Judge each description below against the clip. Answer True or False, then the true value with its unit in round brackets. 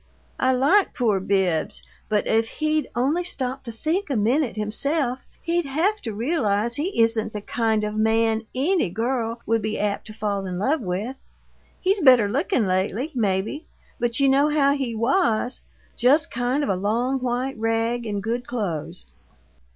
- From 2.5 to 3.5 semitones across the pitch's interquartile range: False (4.4 semitones)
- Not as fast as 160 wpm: False (165 wpm)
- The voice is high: True (235 Hz)